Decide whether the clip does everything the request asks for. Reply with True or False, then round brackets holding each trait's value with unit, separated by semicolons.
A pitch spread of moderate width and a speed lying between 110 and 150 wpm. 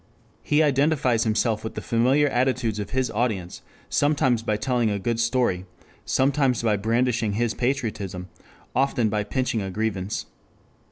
True (3.4 semitones; 145 wpm)